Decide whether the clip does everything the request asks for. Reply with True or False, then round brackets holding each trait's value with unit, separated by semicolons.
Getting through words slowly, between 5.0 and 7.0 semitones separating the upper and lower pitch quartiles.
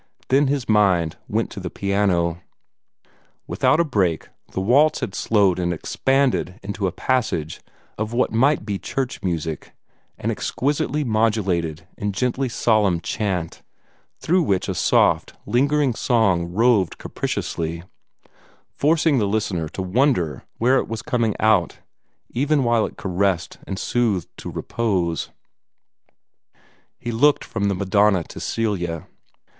True (130 wpm; 5.6 semitones)